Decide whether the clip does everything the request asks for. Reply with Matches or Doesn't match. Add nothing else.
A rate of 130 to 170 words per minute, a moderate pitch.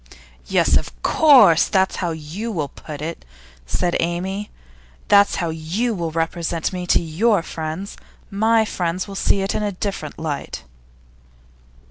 Matches